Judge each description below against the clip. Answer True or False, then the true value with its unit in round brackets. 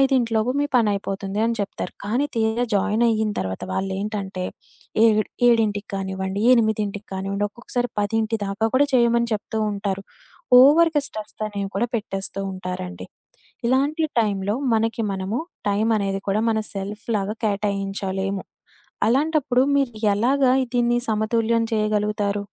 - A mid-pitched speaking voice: False (215 Hz)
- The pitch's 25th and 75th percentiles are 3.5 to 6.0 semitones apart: False (2.9 semitones)